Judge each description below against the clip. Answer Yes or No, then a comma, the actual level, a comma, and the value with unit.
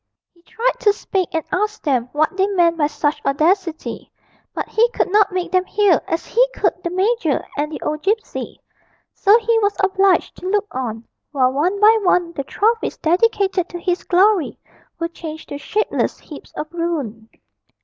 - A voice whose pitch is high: Yes, very high, 360 Hz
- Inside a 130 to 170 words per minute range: No, average, 180 wpm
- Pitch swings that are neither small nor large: Yes, average, 4.8 semitones